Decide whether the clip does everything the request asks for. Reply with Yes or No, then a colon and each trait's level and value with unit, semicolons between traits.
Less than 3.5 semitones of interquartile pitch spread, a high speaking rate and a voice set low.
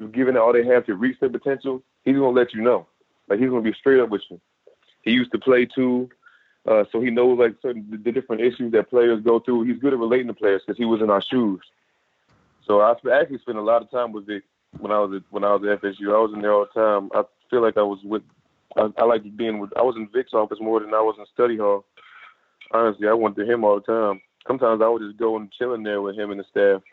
Yes: average, 2.9 semitones; fast, 275 wpm; low, 115 Hz